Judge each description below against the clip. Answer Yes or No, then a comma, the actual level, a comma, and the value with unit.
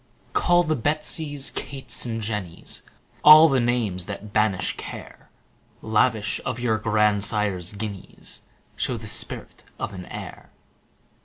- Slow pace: Yes, slow, 130 wpm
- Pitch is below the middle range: Yes, low, 110 Hz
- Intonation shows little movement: No, average, 4.2 semitones